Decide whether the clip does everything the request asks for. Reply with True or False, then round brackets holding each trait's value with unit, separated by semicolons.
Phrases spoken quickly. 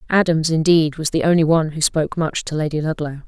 True (220 wpm)